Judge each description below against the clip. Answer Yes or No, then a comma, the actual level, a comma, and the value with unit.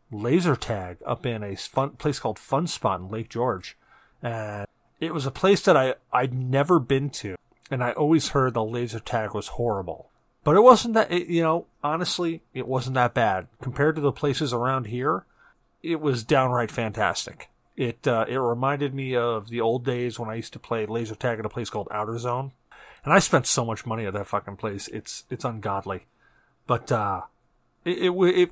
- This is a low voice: Yes, low, 125 Hz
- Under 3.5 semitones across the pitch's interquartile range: No, average, 4.7 semitones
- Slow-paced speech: No, average, 200 wpm